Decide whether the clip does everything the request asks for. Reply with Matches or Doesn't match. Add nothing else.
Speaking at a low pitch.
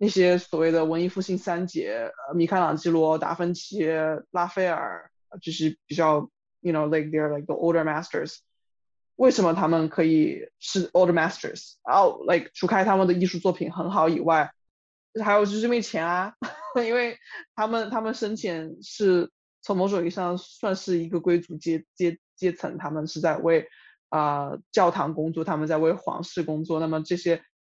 Doesn't match